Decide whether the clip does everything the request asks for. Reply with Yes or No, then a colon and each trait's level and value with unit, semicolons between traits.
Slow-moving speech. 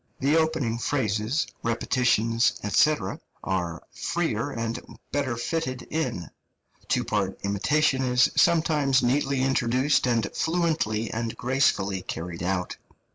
Yes: slow, 110 wpm